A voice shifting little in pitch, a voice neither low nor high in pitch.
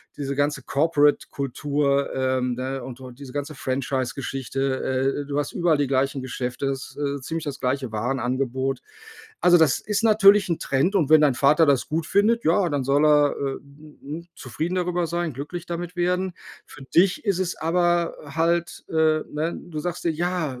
No: average, 4.2 semitones; medium, 145 Hz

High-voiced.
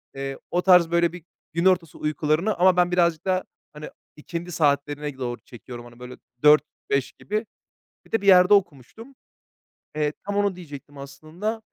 No: medium, 165 Hz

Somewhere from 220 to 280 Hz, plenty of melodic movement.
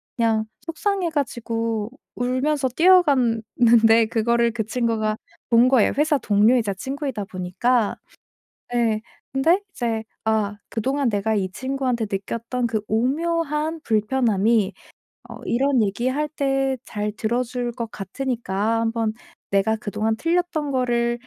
No: high, 235 Hz; average, 3.5 semitones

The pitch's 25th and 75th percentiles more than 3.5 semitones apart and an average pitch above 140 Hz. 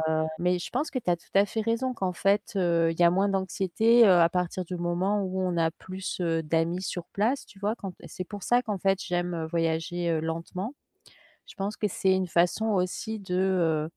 No: average, 2.8 semitones; medium, 185 Hz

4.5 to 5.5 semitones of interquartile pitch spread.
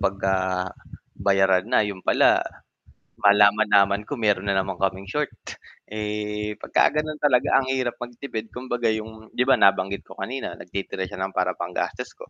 No: average, 3.6 semitones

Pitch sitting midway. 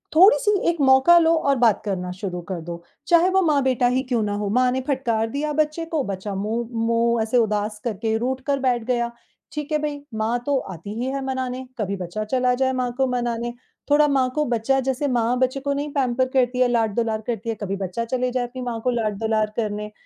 No: high, 245 Hz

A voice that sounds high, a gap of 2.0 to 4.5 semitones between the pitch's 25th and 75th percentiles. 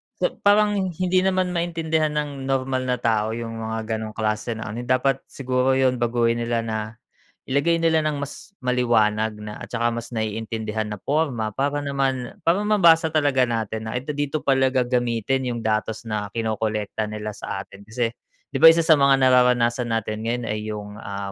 No: low, 120 Hz; average, 4.2 semitones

